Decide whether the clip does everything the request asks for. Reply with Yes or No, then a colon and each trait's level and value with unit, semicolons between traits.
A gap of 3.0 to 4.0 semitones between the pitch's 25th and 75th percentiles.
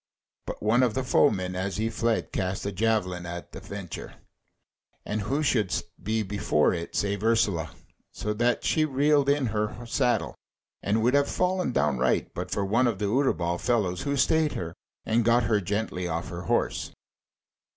No: average, 4.8 semitones